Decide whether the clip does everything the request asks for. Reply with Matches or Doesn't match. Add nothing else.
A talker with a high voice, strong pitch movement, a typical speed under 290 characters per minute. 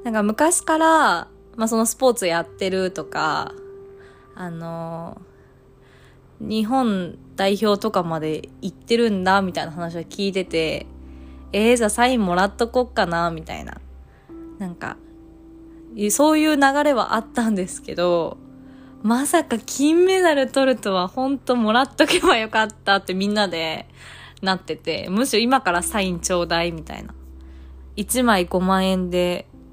Matches